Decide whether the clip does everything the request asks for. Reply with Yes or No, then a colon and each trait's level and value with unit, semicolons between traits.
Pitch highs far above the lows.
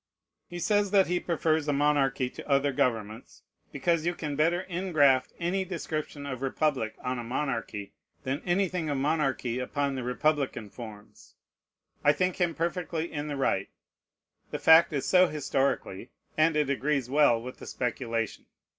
No: average, 4.4 semitones